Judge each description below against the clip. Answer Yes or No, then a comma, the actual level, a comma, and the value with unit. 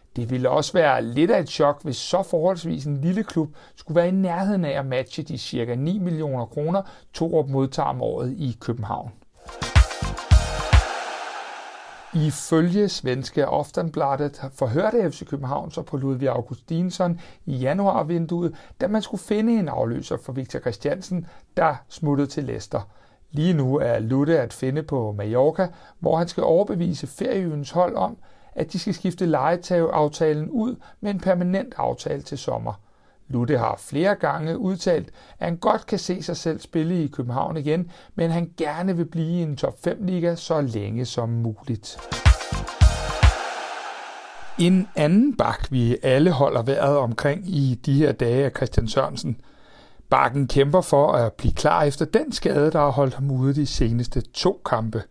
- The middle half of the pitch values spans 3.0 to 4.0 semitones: No, average, 5.1 semitones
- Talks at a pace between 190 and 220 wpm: No, average, 160 wpm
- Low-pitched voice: No, medium, 155 Hz